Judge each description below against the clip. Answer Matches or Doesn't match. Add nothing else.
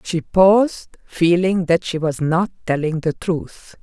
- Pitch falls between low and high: Matches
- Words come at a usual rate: Matches